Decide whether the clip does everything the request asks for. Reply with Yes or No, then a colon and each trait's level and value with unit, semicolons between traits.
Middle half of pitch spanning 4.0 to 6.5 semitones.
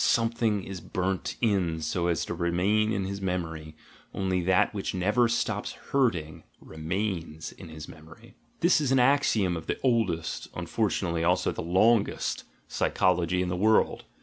Yes: average, 4.3 semitones